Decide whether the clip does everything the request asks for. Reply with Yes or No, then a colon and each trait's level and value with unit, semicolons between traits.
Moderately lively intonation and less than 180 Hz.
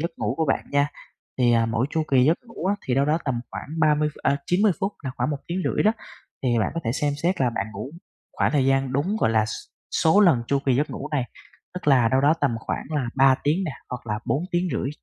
Yes: average, 4.3 semitones; medium, 140 Hz